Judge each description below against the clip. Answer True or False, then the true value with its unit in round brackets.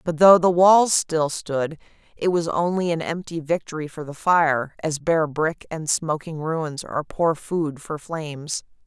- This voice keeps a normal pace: True (175 wpm)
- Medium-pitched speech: True (160 Hz)